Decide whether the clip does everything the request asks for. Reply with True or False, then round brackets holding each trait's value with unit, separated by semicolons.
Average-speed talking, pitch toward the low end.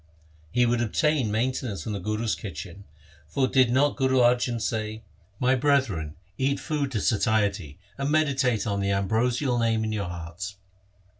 True (165 wpm; 115 Hz)